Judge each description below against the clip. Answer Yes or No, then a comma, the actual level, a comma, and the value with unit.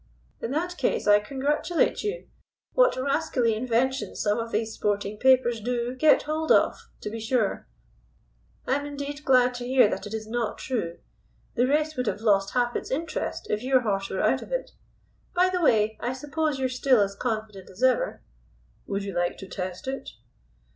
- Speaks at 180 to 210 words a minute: Yes, average, 185 wpm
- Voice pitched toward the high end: Yes, very high, 250 Hz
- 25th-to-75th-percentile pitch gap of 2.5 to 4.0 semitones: No, average, 4.7 semitones